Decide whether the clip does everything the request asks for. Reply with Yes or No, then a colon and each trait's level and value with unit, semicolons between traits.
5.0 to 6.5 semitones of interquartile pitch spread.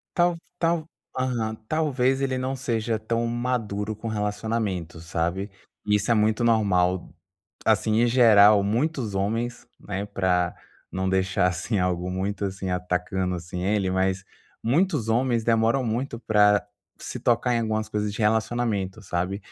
No: average, 3.8 semitones